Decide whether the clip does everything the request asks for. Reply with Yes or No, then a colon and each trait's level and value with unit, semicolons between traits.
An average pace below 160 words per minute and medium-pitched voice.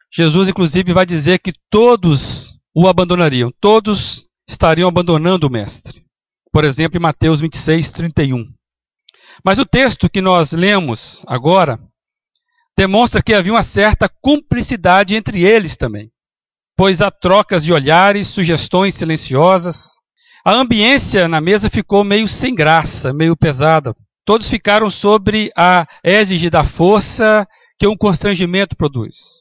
Yes: average, 125 wpm; medium, 180 Hz